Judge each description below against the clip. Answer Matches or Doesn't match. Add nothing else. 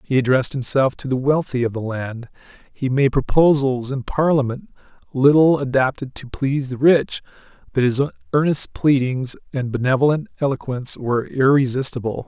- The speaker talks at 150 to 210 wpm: Doesn't match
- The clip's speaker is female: Doesn't match